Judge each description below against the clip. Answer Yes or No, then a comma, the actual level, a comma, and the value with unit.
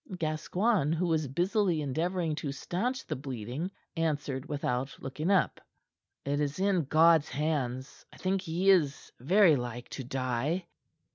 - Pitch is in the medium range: Yes, medium, 155 Hz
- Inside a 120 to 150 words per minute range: Yes, average, 140 wpm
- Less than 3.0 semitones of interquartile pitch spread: No, average, 4.8 semitones